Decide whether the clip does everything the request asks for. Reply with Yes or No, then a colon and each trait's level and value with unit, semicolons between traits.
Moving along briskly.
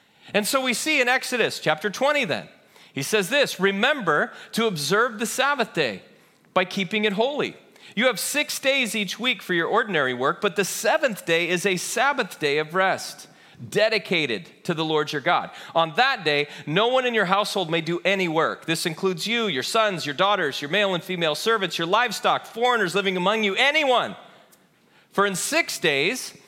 No: average, 190 wpm